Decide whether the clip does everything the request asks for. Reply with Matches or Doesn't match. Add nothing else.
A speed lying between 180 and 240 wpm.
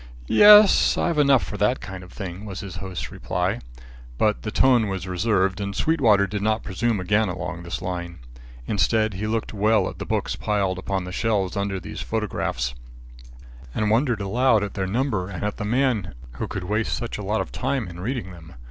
Matches